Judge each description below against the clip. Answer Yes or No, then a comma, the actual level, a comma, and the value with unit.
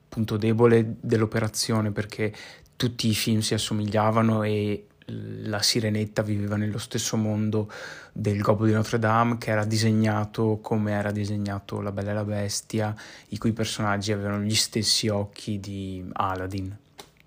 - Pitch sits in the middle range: No, low, 110 Hz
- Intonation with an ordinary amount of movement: No, narrow, 1.3 semitones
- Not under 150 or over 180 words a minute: No, average, 140 wpm